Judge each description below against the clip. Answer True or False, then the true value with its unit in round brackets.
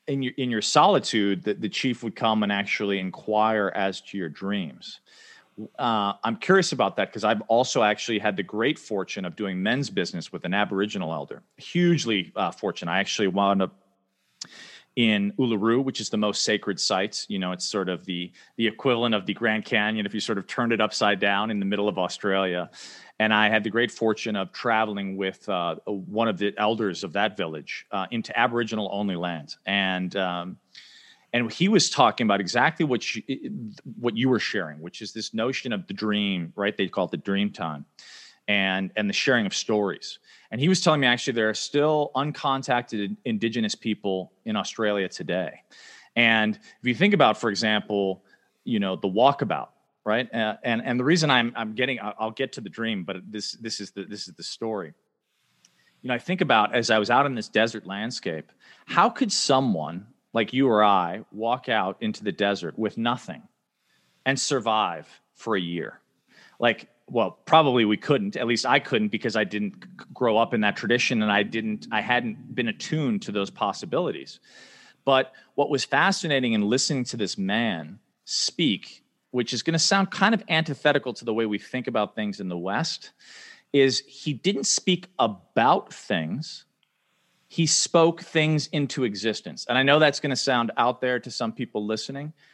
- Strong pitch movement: False (4.3 semitones)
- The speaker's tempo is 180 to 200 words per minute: True (190 wpm)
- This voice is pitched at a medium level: False (110 Hz)